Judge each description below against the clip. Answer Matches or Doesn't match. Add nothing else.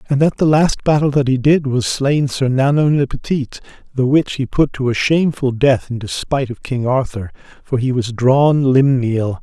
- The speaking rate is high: Matches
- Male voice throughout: Matches